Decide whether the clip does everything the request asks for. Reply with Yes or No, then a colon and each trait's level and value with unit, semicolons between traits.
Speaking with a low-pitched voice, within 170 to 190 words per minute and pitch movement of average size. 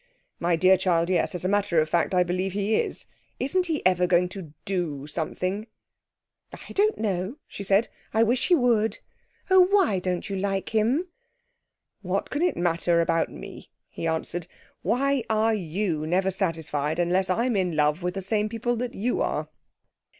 No: high, 190 Hz; average, 175 wpm; average, 4.4 semitones